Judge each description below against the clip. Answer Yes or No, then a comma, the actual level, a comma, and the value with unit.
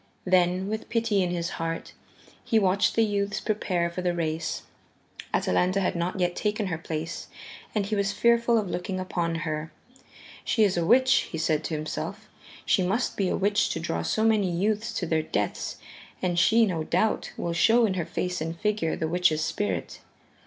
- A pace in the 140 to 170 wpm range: No, average, 190 wpm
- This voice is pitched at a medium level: Yes, medium, 180 Hz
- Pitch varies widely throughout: No, average, 4.0 semitones